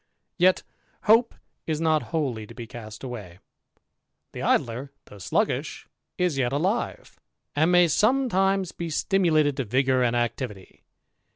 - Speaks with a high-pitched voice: No, medium, 145 Hz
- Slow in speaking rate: Yes, slow, 130 wpm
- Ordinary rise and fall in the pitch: No, wide, 6.8 semitones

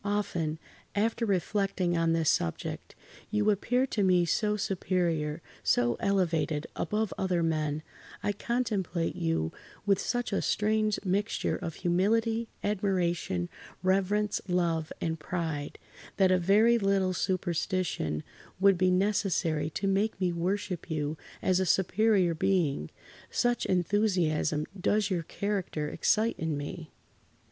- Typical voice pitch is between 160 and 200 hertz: Yes, medium, 185 Hz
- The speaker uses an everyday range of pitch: Yes, average, 3.9 semitones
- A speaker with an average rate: No, slow, 125 wpm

